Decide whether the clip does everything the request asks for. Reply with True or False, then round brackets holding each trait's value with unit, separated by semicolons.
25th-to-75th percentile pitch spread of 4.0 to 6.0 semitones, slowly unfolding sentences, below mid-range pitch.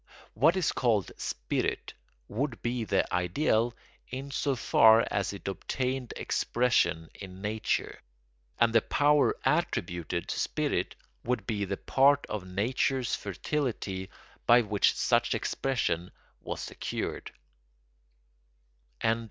True (5.3 semitones; 110 wpm; 115 Hz)